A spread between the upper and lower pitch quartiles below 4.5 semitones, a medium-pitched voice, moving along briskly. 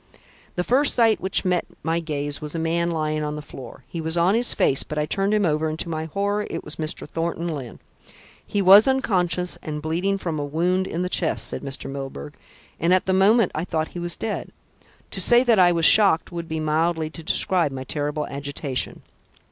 Yes: average, 3.6 semitones; medium, 165 Hz; fast, 215 wpm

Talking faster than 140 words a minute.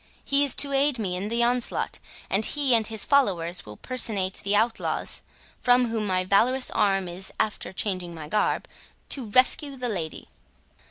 Yes: average, 170 wpm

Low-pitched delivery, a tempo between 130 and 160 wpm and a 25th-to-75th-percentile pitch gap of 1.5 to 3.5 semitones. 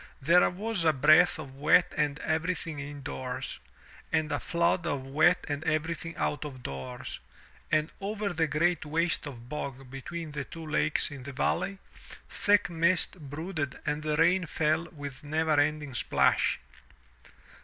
No: medium, 155 Hz; average, 155 wpm; average, 2.9 semitones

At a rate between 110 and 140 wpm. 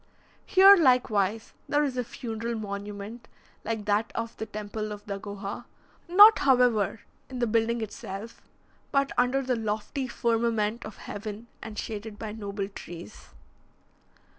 Yes: slow, 135 wpm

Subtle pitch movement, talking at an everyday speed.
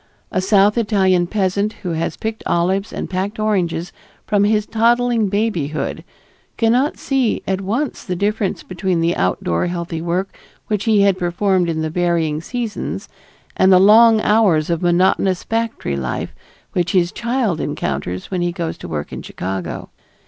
No: average, 3.8 semitones; average, 155 wpm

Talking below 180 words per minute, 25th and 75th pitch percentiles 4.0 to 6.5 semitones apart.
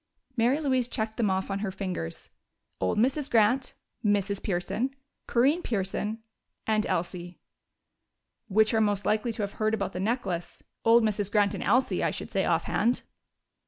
No: average, 160 wpm; average, 3.3 semitones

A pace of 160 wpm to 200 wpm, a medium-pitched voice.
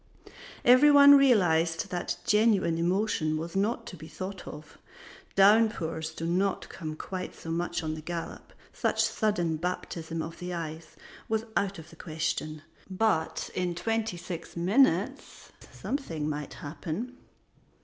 No: average, 140 wpm; medium, 175 Hz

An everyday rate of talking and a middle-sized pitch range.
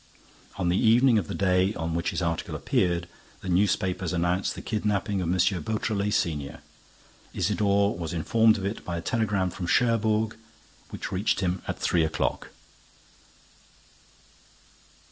Yes: average, 145 wpm; average, 3.3 semitones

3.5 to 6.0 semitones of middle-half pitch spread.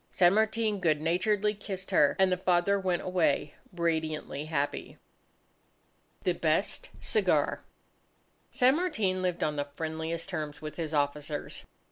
Yes: average, 4.1 semitones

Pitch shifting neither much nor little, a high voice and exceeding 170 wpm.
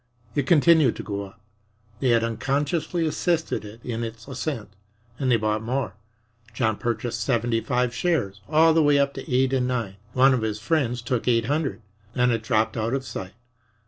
No: average, 3.8 semitones; low, 125 Hz; average, 185 wpm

